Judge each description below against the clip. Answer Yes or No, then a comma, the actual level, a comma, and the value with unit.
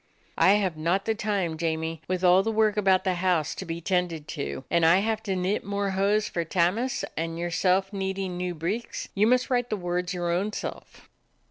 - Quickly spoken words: Yes, fast, 210 wpm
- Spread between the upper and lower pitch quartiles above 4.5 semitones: No, average, 3.0 semitones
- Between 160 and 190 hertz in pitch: Yes, medium, 185 Hz